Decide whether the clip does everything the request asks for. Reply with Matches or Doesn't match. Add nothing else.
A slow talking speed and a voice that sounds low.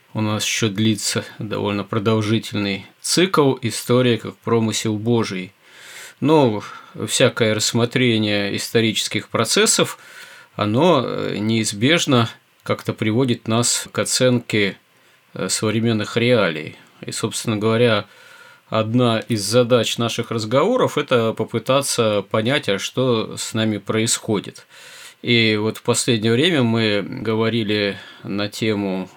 Matches